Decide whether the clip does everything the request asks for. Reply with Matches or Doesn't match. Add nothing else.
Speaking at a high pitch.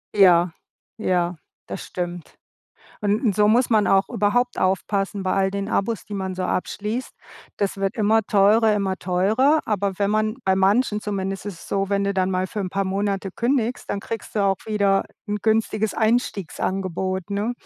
Matches